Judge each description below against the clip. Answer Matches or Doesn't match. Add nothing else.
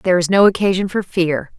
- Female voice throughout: Matches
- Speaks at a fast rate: Matches